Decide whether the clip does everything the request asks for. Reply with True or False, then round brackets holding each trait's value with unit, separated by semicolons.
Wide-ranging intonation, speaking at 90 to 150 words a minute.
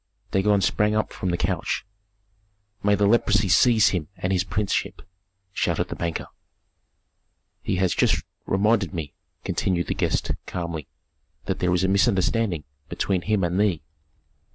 False (2.8 semitones; 145 wpm)